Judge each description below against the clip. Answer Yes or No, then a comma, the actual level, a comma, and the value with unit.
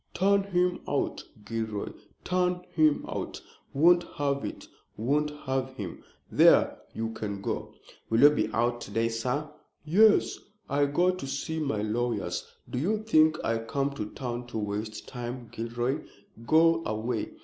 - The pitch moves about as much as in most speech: No, wide, 5.8 semitones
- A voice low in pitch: Yes, low, 130 Hz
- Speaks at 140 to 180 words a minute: Yes, average, 150 wpm